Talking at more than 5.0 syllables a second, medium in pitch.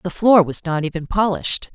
Yes: 5.7 syllables/s; medium, 180 Hz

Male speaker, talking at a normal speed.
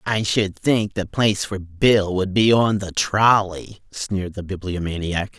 Yes: male; average, 165 wpm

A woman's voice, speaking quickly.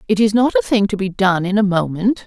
Yes: female; fast, 290 wpm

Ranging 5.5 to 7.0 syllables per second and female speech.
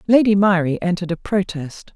Yes: 5.6 syllables/s; female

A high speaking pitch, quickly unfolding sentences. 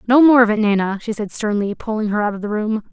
Yes: high, 215 Hz; fast, 290 wpm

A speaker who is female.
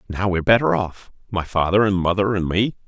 No: male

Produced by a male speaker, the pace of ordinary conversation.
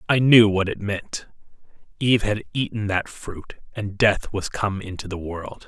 Yes: male; average, 170 wpm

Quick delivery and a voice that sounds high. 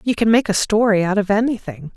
Yes: fast, 245 wpm; high, 210 Hz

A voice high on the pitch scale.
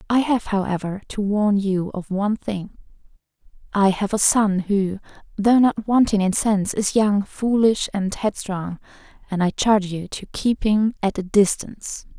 Yes: high, 205 Hz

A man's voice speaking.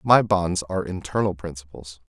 Yes: male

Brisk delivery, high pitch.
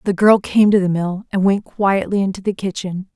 Yes: fast, 230 wpm; high, 195 Hz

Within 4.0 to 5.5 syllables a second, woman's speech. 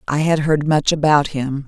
Yes: 4.6 syllables/s; female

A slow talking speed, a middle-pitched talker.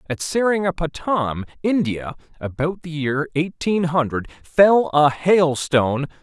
Yes: slow, 105 wpm; medium, 160 Hz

